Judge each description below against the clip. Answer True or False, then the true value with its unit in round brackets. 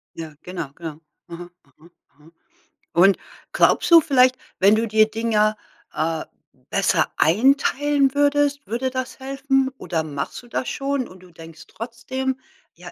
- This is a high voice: True (225 Hz)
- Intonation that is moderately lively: False (7.8 semitones)